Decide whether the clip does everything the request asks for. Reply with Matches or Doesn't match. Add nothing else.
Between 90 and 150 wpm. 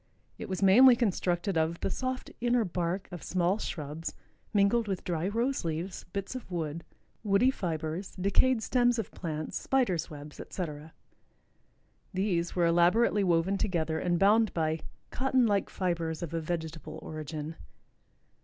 Matches